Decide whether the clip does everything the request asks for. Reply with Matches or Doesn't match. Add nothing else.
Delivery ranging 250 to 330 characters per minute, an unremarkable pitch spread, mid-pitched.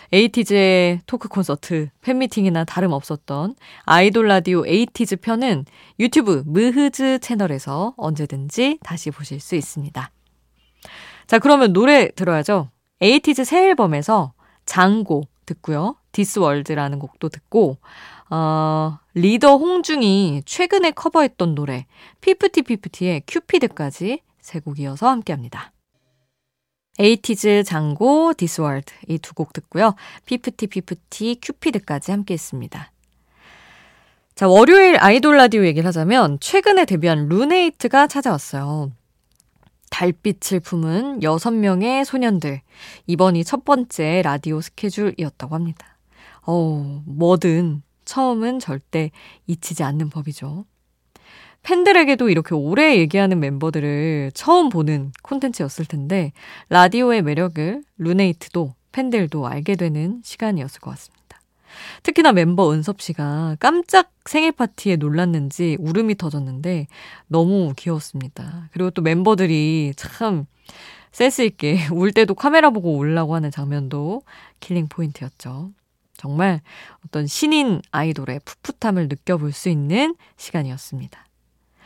Doesn't match